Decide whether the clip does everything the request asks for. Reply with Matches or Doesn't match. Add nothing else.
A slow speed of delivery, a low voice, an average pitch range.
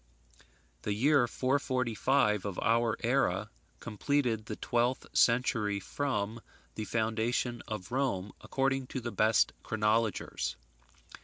Matches